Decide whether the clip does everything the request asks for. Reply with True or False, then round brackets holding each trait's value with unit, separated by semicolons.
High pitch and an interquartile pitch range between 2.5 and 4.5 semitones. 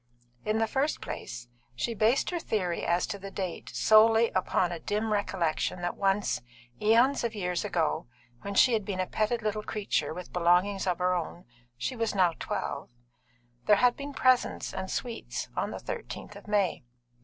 True (205 Hz; 3.8 semitones)